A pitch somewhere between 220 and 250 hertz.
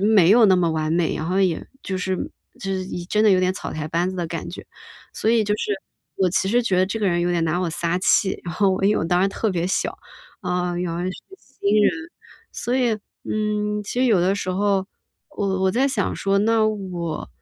No: high, 190 Hz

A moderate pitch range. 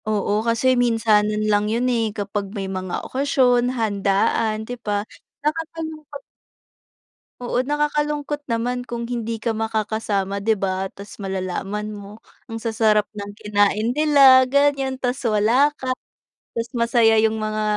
Yes: average, 3.4 semitones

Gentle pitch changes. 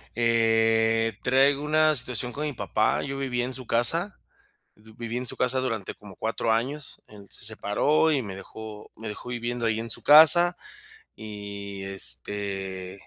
No: average, 3.9 semitones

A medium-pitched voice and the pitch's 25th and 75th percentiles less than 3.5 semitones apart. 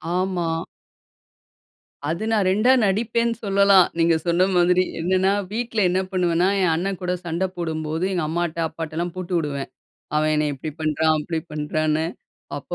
Yes: medium, 175 Hz; average, 3.0 semitones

